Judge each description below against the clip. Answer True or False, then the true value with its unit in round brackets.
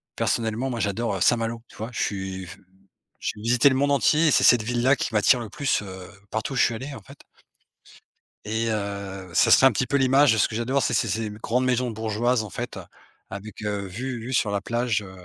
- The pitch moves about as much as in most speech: True (3.5 semitones)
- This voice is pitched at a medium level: False (115 Hz)